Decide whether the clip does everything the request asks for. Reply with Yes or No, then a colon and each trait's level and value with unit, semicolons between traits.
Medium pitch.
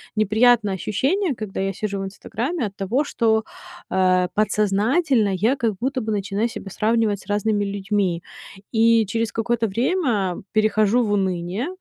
No: high, 215 Hz